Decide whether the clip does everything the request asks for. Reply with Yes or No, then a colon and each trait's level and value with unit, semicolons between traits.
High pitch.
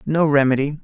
No: medium, 145 Hz